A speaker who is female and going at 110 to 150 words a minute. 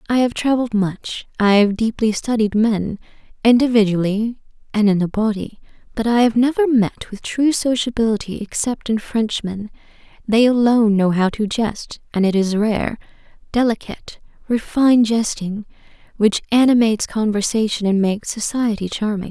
Yes: female; average, 140 wpm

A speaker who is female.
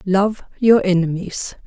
Yes: female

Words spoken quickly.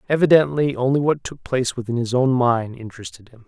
No: average, 190 wpm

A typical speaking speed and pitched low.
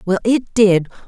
No: average, 165 wpm; high, 205 Hz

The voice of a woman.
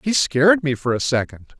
No: male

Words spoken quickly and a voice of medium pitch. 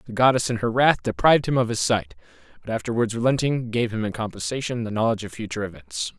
No: fast, 215 wpm; low, 115 Hz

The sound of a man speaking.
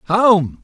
Yes: male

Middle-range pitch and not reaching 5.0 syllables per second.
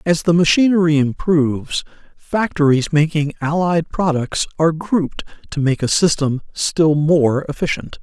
Yes: medium, 160 Hz; 4.6 syllables/s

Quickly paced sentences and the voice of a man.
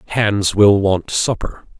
No: slow, 135 wpm; male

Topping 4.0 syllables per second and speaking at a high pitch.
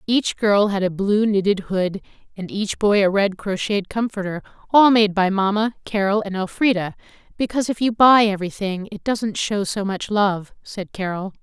No: 3.3 syllables/s; high, 205 Hz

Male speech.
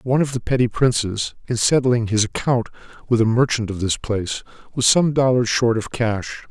Yes: male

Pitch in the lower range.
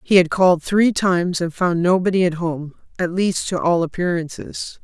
No: medium, 175 Hz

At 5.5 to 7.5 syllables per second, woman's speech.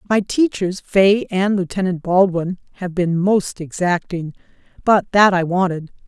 No: 4.2 syllables/s; female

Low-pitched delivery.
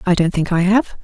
No: medium, 185 Hz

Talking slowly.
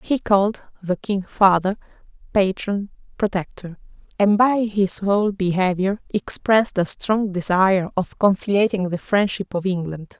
Yes: slow, 130 wpm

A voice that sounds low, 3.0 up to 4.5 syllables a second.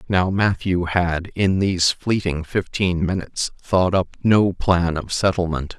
Yes: very low, 90 Hz; 4.1 syllables/s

